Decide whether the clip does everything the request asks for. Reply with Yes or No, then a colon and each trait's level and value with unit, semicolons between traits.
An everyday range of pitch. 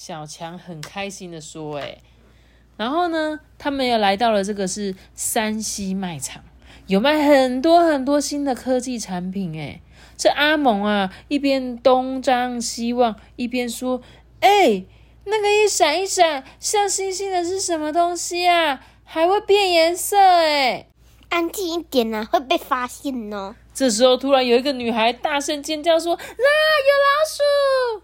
No: wide, 7.5 semitones